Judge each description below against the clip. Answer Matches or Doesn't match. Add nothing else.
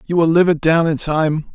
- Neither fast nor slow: Doesn't match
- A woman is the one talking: Doesn't match